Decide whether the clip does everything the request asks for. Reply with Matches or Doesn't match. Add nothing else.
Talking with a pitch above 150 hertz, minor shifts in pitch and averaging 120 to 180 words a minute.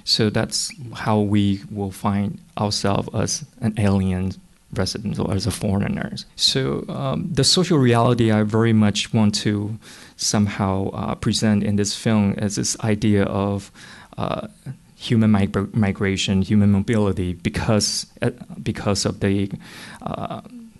Doesn't match